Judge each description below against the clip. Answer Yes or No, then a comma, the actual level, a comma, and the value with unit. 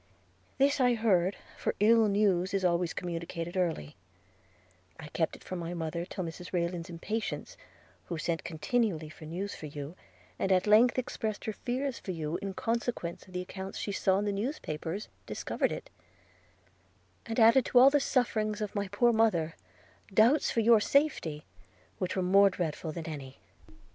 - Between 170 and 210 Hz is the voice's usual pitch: Yes, high, 190 Hz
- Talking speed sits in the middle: Yes, average, 170 wpm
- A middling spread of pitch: Yes, average, 4.9 semitones